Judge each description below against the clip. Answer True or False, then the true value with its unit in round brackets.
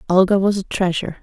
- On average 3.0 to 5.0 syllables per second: False (7.0 syllables/s)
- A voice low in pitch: False (185 Hz)